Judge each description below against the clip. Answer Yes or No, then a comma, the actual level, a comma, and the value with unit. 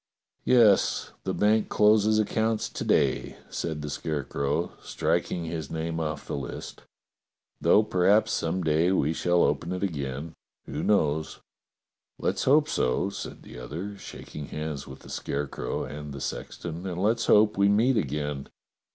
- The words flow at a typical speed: Yes, average, 155 wpm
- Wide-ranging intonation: Yes, wide, 5.8 semitones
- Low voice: Yes, very low, 85 Hz